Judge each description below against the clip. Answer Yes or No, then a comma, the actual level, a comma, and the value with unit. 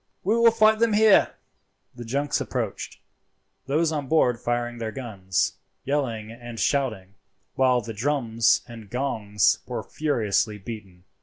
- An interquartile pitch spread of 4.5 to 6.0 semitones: Yes, average, 4.9 semitones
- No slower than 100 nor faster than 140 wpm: Yes, slow, 135 wpm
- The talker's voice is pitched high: No, low, 120 Hz